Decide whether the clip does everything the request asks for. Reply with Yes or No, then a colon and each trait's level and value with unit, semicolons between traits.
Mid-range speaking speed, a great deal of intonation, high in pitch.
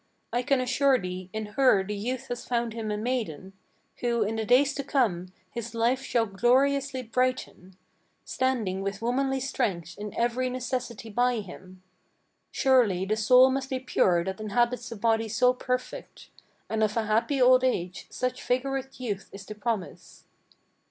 No: average, 165 wpm; average, 3.6 semitones; high, 235 Hz